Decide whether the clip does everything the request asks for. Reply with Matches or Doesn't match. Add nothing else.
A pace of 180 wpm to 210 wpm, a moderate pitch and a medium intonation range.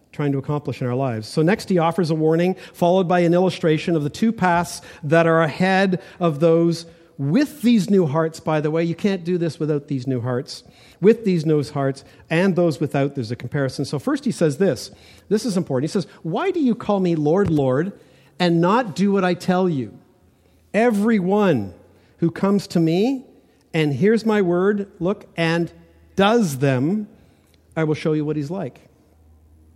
Matches